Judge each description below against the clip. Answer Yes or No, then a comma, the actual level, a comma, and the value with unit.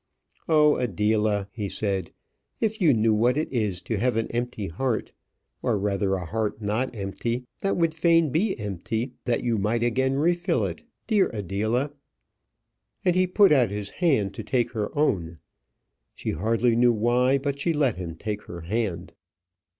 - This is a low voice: Yes, low, 115 Hz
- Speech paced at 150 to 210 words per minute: Yes, average, 165 wpm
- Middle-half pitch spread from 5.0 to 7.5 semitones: Yes, average, 5.3 semitones